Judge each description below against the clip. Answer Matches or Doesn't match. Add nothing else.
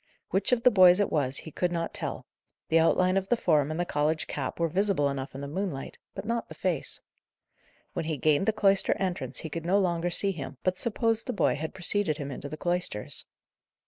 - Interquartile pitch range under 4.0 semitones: Doesn't match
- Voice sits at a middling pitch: Matches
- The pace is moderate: Doesn't match